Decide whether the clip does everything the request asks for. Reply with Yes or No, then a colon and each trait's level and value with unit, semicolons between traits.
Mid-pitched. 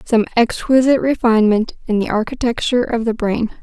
No: high, 230 Hz